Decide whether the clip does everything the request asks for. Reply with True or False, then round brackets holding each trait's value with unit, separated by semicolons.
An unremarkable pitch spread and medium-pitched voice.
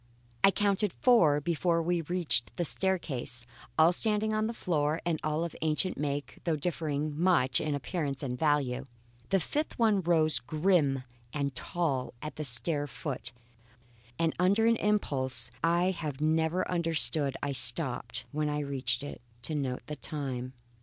True (3.9 semitones; 155 Hz)